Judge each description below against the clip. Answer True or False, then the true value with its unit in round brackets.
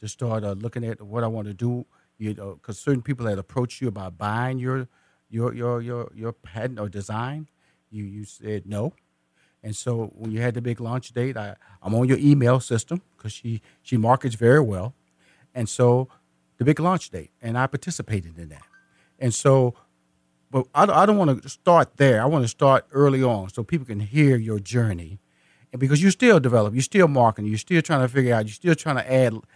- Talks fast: True (215 wpm)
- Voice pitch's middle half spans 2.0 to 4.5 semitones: True (3.8 semitones)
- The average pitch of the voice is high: False (120 Hz)